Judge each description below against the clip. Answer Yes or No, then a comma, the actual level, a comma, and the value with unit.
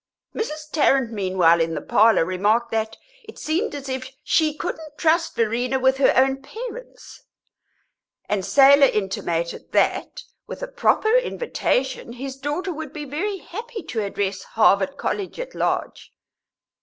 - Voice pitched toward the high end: Yes, very high, 270 Hz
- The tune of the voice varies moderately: No, wide, 6.7 semitones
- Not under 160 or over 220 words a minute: No, average, 145 wpm